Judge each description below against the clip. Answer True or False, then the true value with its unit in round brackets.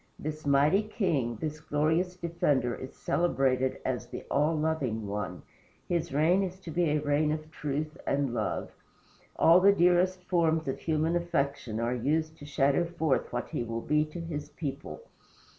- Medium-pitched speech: True (155 Hz)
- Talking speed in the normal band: True (165 wpm)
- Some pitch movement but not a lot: True (3.8 semitones)